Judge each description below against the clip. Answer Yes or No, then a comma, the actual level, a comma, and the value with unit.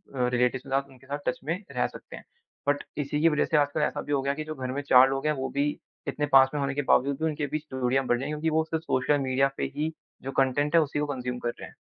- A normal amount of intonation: No, narrow, 2.2 semitones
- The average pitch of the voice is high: No, medium, 140 Hz